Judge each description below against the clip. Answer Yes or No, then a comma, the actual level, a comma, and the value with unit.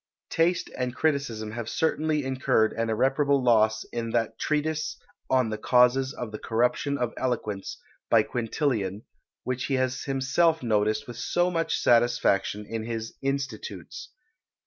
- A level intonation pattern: No, average, 3.8 semitones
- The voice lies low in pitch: Yes, low, 125 Hz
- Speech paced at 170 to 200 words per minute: No, average, 140 wpm